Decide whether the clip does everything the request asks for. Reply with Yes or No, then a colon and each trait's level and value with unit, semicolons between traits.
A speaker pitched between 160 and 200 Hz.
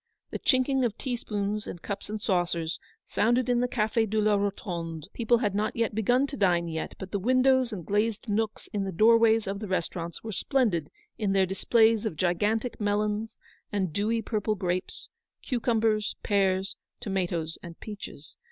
No: high, 210 Hz